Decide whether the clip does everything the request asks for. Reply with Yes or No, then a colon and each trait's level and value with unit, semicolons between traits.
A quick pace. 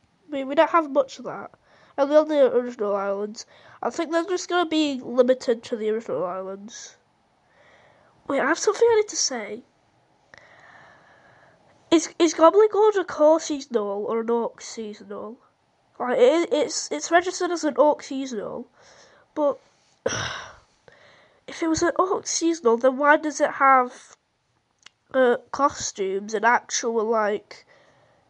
No: average, 150 wpm